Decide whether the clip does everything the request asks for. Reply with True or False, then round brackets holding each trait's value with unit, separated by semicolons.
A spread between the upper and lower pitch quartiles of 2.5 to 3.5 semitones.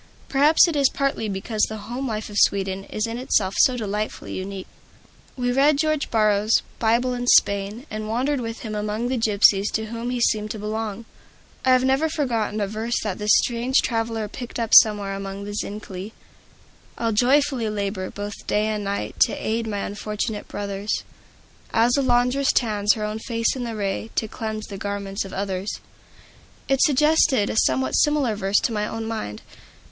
True (3.1 semitones)